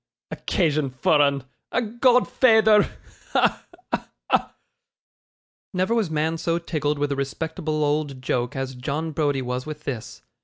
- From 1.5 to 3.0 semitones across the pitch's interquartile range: No, average, 3.8 semitones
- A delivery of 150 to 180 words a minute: No, average, 140 wpm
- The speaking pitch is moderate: Yes, medium, 150 Hz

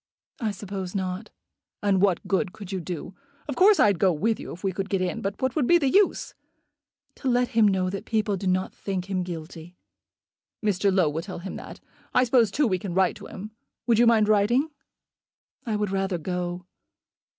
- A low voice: No, high, 195 Hz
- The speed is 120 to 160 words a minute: No, fast, 205 wpm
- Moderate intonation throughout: Yes, average, 3.4 semitones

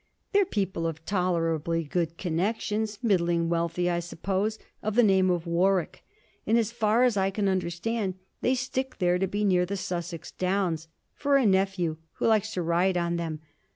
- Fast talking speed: No, average, 175 wpm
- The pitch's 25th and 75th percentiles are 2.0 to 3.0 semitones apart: No, average, 3.6 semitones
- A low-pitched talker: No, medium, 185 Hz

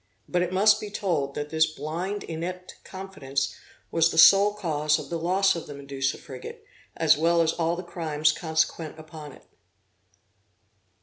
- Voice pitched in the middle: Yes, medium, 165 Hz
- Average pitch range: Yes, average, 3.1 semitones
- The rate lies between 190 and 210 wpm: No, average, 165 wpm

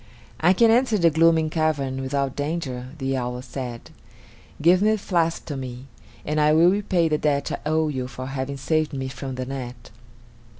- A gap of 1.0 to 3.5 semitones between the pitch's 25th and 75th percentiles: No, average, 3.9 semitones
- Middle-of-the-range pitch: Yes, medium, 145 Hz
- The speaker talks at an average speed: Yes, average, 180 wpm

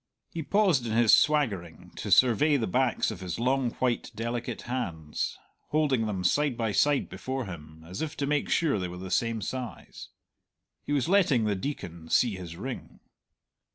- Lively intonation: Yes, wide, 6.8 semitones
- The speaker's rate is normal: Yes, average, 175 wpm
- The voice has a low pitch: Yes, low, 120 Hz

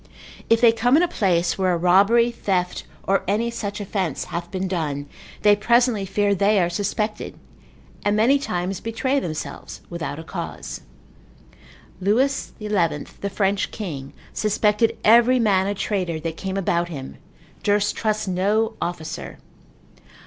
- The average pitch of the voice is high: Yes, high, 200 Hz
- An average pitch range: Yes, average, 3.7 semitones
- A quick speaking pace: No, average, 145 wpm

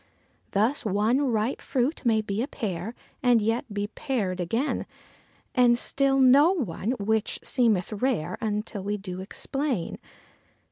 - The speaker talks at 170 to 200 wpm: No, slow, 135 wpm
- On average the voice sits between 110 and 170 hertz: No, high, 225 Hz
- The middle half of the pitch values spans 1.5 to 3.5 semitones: No, average, 4.0 semitones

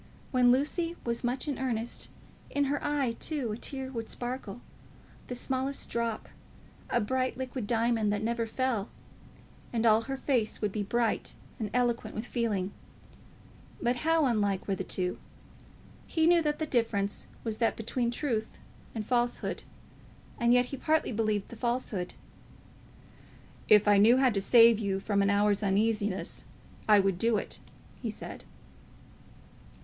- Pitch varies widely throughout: No, average, 3.4 semitones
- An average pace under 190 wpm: Yes, average, 155 wpm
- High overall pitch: Yes, high, 235 Hz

